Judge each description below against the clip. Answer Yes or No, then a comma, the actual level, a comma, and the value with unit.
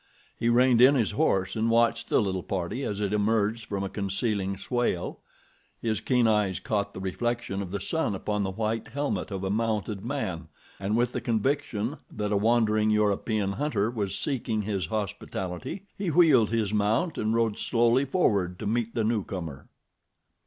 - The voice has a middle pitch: No, low, 110 Hz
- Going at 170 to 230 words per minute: Yes, average, 175 wpm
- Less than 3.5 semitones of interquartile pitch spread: Yes, average, 3.0 semitones